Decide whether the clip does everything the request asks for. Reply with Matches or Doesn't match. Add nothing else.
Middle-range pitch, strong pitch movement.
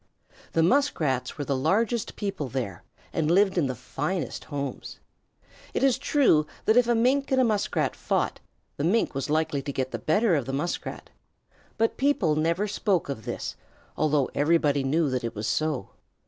Matches